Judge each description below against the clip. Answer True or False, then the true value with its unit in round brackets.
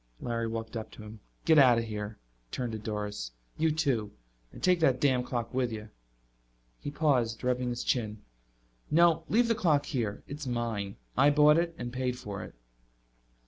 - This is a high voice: False (125 Hz)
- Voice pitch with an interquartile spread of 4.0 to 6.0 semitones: True (5.0 semitones)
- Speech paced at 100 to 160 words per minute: False (185 wpm)